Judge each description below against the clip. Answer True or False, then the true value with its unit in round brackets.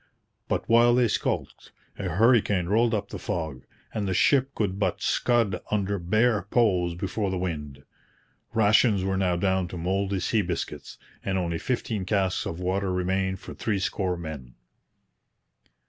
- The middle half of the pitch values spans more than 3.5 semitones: False (3.0 semitones)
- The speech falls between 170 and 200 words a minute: False (155 wpm)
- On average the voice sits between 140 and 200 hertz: False (95 Hz)